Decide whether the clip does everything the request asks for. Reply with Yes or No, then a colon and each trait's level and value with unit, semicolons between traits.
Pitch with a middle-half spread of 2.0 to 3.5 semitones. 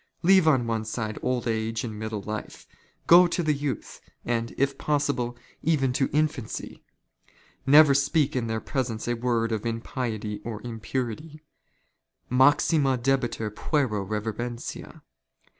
No: average, 4.1 semitones